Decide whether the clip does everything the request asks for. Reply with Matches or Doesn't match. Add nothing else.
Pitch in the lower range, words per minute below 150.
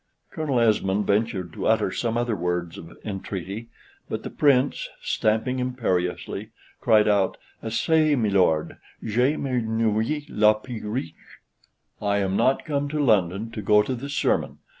Matches